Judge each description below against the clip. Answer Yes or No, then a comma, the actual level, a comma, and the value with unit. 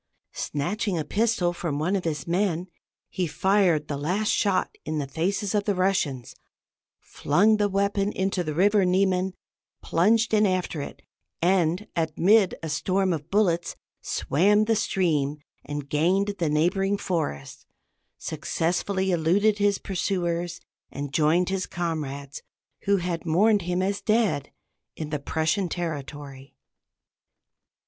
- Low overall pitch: No, medium, 180 Hz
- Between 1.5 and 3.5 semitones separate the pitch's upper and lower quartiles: No, average, 4.1 semitones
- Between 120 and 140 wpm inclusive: Yes, slow, 135 wpm